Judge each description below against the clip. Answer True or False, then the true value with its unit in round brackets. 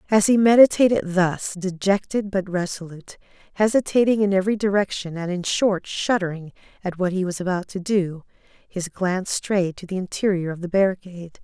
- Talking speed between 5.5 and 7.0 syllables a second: False (5.3 syllables/s)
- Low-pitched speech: False (190 Hz)